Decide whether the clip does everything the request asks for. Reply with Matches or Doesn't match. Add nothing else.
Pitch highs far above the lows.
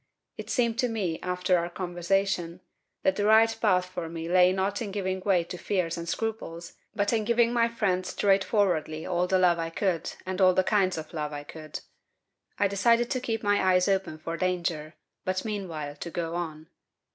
Doesn't match